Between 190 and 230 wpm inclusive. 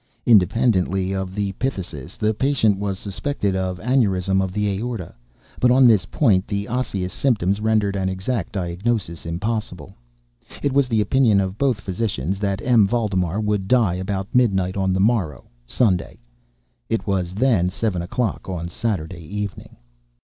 No: average, 150 wpm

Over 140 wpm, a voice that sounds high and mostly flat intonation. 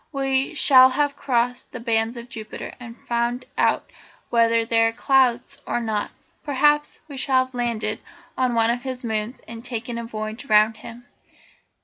Yes: average, 165 wpm; high, 240 Hz; narrow, 2.3 semitones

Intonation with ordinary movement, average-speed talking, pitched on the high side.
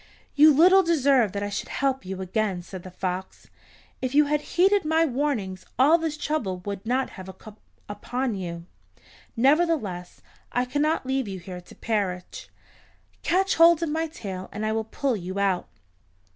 No: wide, 8.0 semitones; average, 170 wpm; high, 240 Hz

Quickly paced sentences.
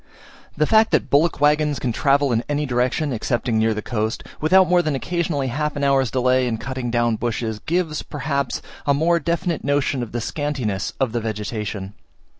No: average, 185 wpm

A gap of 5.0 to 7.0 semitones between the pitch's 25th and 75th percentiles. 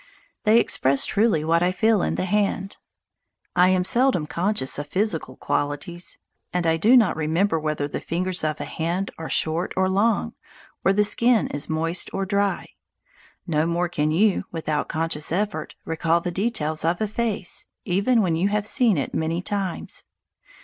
No: average, 4.1 semitones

